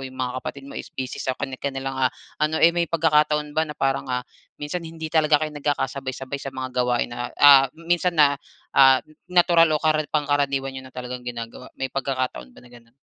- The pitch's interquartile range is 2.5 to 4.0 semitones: Yes, average, 2.9 semitones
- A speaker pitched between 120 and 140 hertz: Yes, low, 135 Hz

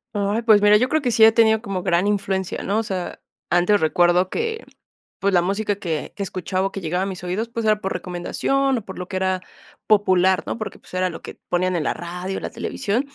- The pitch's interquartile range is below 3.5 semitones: Yes, average, 3.1 semitones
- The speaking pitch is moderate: No, high, 195 Hz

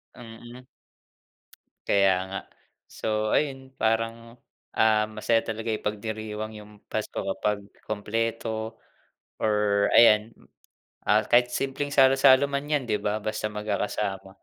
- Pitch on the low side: Yes, low, 110 Hz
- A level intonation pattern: Yes, narrow, 2.1 semitones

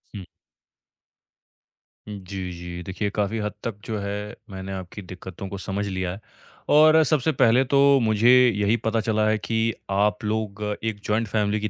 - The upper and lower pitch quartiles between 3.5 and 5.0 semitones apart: No, narrow, 2.4 semitones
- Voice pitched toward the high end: No, low, 105 Hz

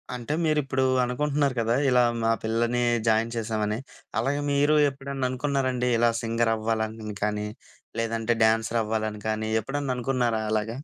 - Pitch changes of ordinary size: Yes, average, 3.1 semitones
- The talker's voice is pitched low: Yes, low, 115 Hz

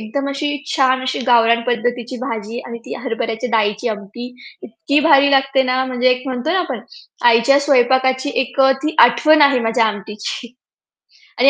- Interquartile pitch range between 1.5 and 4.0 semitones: Yes, average, 2.9 semitones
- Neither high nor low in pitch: No, very high, 250 Hz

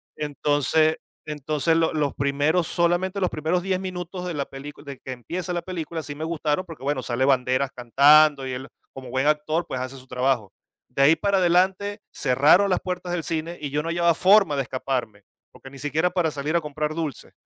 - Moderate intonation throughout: Yes, average, 4.0 semitones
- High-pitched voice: No, medium, 155 Hz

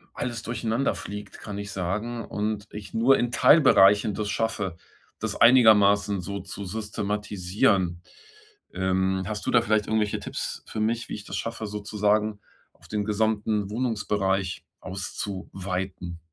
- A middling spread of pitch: No, narrow, 2.1 semitones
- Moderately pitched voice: No, low, 105 Hz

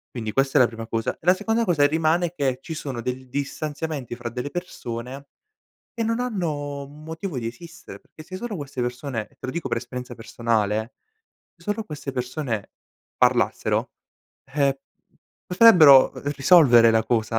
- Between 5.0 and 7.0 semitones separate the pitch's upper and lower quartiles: Yes, average, 5.3 semitones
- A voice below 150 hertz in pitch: Yes, medium, 140 Hz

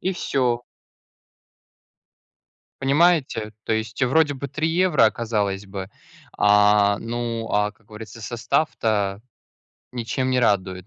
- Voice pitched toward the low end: Yes, low, 115 Hz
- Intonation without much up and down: No, average, 4.3 semitones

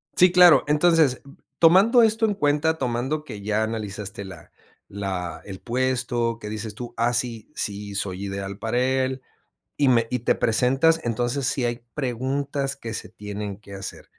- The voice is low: Yes, low, 120 Hz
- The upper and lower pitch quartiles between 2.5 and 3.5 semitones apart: No, average, 5.1 semitones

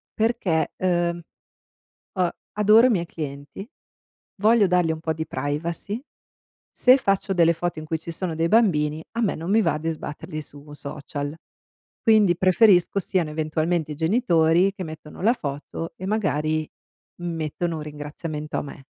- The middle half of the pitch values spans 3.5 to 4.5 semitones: Yes, average, 3.9 semitones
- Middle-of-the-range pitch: Yes, medium, 165 Hz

